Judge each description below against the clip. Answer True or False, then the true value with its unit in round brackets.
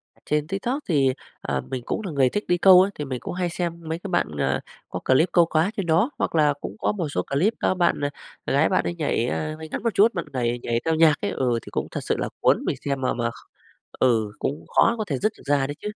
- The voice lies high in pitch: False (155 Hz)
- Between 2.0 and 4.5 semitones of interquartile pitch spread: False (5.3 semitones)